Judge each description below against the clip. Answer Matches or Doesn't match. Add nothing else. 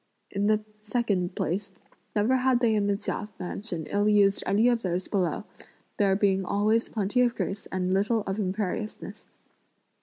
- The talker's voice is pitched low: Doesn't match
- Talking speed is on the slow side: Doesn't match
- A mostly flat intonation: Matches